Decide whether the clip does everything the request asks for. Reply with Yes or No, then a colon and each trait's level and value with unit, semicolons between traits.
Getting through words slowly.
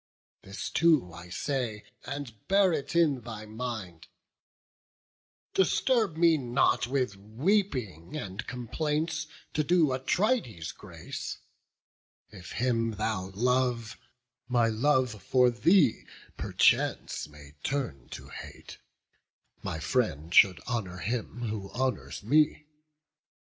Yes: slow, 110 wpm